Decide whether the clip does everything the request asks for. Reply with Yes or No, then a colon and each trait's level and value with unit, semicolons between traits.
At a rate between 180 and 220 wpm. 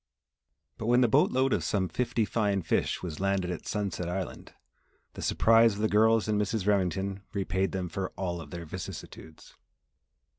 No: average, 170 wpm